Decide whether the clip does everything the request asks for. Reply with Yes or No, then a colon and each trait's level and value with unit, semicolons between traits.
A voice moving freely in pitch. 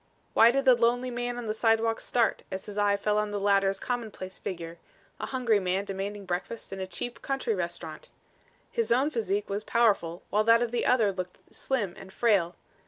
No: average, 3.7 semitones